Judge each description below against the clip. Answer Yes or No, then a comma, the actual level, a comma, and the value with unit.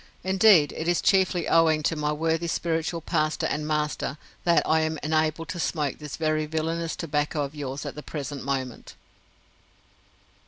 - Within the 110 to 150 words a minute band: No, average, 160 wpm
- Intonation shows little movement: Yes, narrow, 1.7 semitones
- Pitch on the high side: No, medium, 155 Hz